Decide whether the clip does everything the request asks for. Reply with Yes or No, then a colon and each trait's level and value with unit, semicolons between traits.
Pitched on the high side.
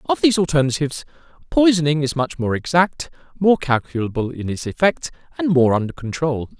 No: medium, 150 Hz